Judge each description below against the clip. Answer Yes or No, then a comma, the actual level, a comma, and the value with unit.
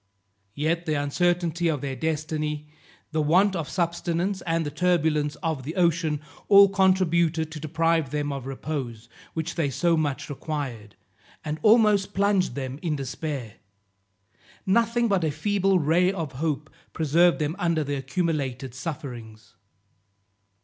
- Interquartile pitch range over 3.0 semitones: Yes, average, 3.5 semitones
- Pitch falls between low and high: Yes, medium, 160 Hz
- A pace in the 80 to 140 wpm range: Yes, slow, 135 wpm